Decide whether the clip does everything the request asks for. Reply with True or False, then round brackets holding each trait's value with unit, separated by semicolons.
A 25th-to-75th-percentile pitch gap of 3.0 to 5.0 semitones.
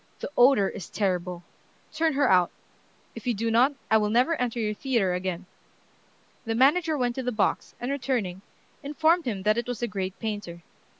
False (5.4 semitones)